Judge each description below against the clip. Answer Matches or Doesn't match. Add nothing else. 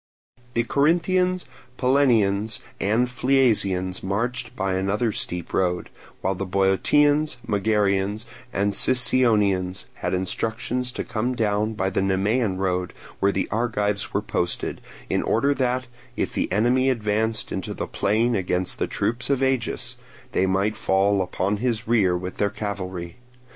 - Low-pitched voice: Matches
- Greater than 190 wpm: Doesn't match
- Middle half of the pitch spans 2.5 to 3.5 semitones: Doesn't match